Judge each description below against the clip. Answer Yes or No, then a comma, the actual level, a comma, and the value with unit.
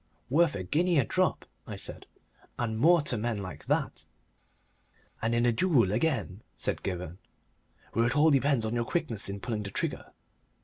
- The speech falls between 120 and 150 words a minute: No, average, 175 wpm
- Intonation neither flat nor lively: No, wide, 6.3 semitones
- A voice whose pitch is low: Yes, low, 115 Hz